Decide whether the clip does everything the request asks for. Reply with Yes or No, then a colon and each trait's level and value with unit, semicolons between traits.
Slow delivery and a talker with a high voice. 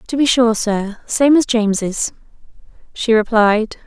Yes: slow, 125 wpm; high, 225 Hz